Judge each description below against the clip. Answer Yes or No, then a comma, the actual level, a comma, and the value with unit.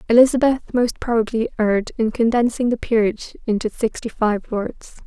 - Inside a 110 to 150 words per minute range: Yes, average, 140 wpm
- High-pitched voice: Yes, high, 230 Hz